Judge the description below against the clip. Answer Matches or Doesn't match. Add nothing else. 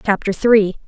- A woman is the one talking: Matches